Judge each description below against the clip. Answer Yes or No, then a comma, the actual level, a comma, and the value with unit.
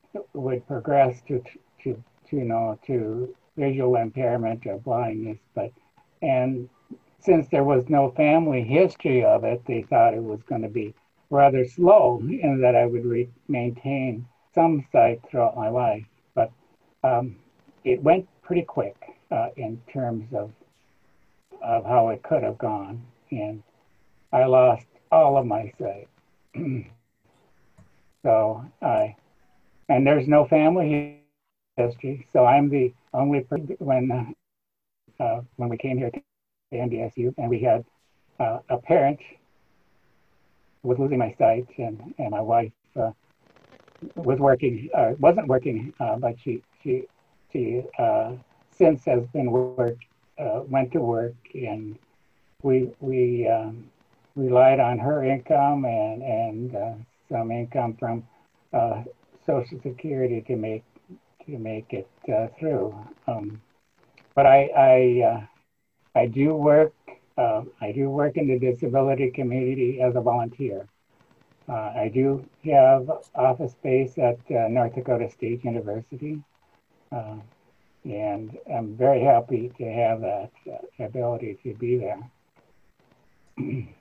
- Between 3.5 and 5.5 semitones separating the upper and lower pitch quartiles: No, average, 3.1 semitones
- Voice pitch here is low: Yes, low, 125 Hz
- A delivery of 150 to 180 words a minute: No, slow, 135 wpm